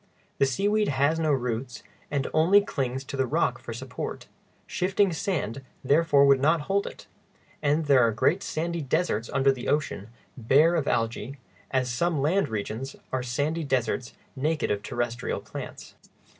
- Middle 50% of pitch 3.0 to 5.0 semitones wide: Yes, average, 4.6 semitones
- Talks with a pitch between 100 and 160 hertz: Yes, medium, 140 Hz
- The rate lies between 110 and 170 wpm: Yes, average, 155 wpm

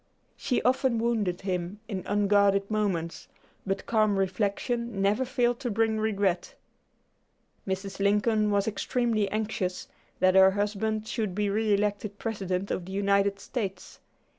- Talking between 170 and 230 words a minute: No, slow, 135 wpm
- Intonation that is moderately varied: No, narrow, 2.2 semitones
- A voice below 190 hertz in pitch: No, high, 205 Hz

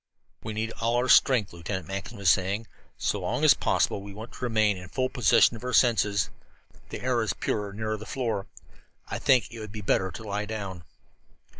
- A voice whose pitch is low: Yes, low, 110 Hz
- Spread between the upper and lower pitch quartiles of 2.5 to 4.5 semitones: Yes, average, 3.0 semitones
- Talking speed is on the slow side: No, average, 200 wpm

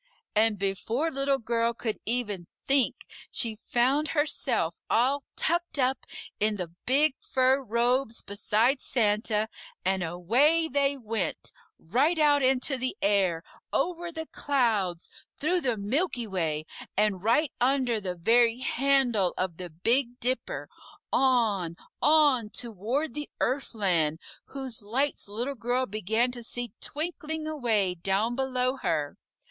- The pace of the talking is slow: Yes, slow, 130 wpm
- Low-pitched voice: No, high, 240 Hz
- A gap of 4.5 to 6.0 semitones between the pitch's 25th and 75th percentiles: Yes, average, 4.8 semitones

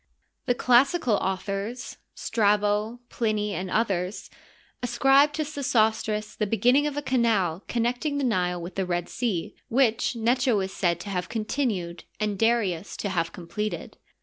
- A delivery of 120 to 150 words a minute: Yes, average, 140 wpm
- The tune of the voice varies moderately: Yes, average, 4.4 semitones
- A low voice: No, high, 215 Hz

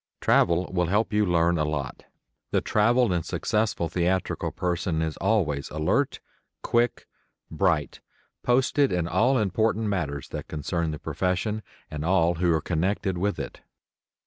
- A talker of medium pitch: No, very low, 90 Hz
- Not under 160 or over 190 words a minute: No, average, 145 wpm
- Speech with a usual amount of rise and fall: Yes, average, 4.6 semitones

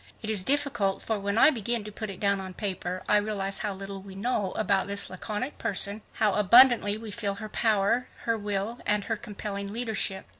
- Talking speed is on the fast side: Yes, fast, 215 wpm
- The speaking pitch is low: No, high, 205 Hz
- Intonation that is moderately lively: No, narrow, 2.0 semitones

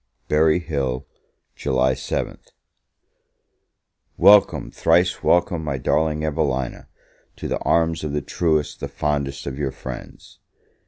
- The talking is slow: Yes, slow, 115 wpm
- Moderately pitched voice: No, very low, 75 Hz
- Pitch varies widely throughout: No, average, 3.0 semitones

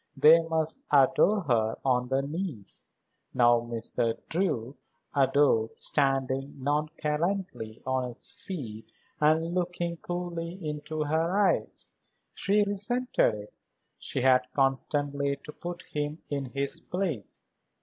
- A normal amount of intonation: Yes, average, 4.5 semitones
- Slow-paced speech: Yes, slow, 115 wpm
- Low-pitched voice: No, medium, 150 Hz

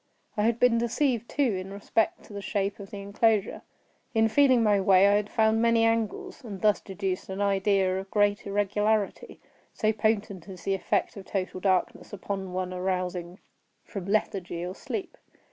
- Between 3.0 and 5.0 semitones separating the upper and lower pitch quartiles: No, narrow, 2.5 semitones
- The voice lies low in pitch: No, high, 200 Hz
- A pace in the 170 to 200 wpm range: Yes, average, 175 wpm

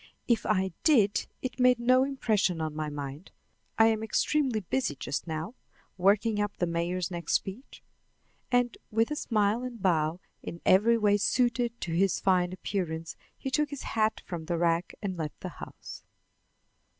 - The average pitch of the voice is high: Yes, high, 200 Hz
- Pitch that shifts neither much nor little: No, wide, 5.7 semitones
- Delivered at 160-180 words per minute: Yes, average, 165 wpm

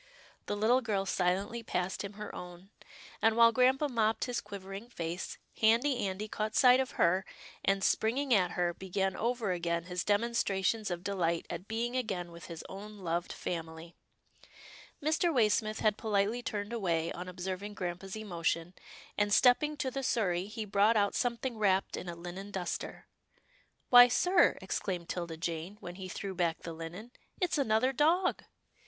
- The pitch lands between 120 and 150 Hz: No, high, 200 Hz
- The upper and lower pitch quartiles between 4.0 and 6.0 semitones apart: Yes, average, 4.6 semitones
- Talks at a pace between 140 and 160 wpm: No, average, 170 wpm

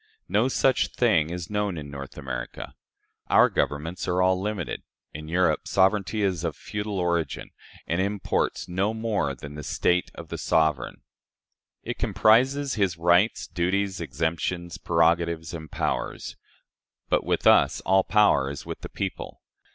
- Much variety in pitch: No, average, 4.0 semitones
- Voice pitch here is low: Yes, very low, 90 Hz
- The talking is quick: No, average, 145 wpm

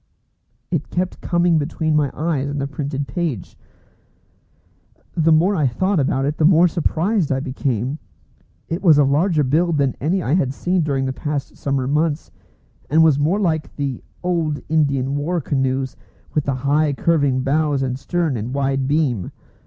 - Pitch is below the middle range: No, medium, 145 Hz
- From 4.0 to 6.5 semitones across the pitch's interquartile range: No, average, 3.3 semitones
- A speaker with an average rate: Yes, average, 170 wpm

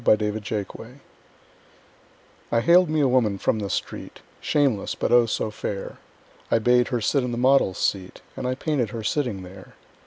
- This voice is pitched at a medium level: No, low, 115 Hz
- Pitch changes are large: No, average, 3.6 semitones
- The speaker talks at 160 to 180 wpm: Yes, average, 175 wpm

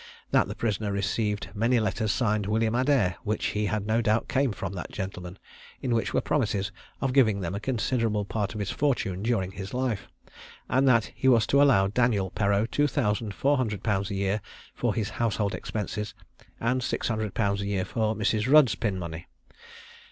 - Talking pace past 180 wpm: Yes, average, 190 wpm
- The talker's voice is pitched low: Yes, low, 110 Hz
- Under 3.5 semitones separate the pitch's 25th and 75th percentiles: Yes, average, 2.8 semitones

